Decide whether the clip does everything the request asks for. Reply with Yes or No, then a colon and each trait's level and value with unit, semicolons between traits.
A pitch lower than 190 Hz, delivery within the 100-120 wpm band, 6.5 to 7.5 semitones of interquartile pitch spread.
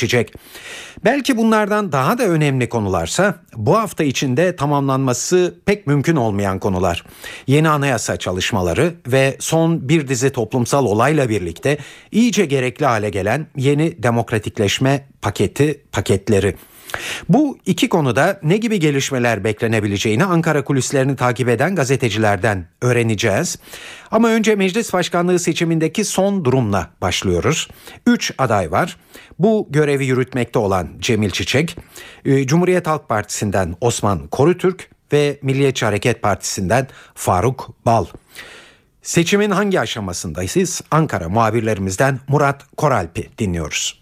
Yes: low, 135 Hz; average, 110 wpm; wide, 7.1 semitones